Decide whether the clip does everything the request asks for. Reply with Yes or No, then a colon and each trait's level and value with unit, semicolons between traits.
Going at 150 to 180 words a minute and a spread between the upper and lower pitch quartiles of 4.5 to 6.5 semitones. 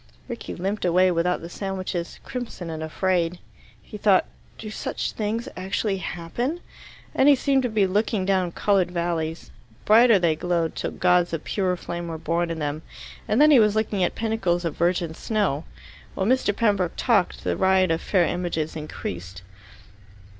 No: average, 170 wpm; average, 3.9 semitones